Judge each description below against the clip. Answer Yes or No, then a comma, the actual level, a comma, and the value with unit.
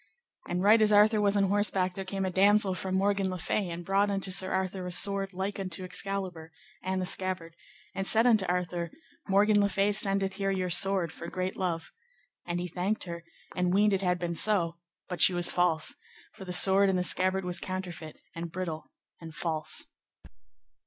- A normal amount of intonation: No, narrow, 1.8 semitones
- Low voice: No, medium, 185 Hz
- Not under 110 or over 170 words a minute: No, average, 195 wpm